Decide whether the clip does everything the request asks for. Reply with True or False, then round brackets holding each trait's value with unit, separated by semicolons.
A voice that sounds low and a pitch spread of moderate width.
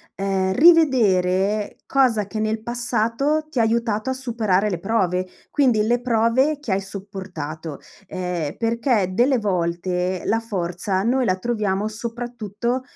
False (215 Hz; 4.2 semitones)